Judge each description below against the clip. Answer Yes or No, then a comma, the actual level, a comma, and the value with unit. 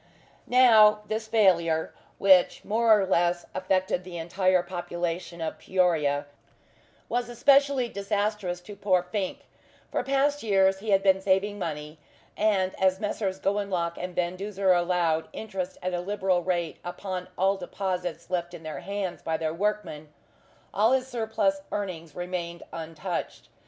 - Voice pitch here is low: No, medium, 185 Hz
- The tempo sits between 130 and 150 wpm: Yes, average, 140 wpm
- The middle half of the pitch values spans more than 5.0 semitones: No, average, 3.0 semitones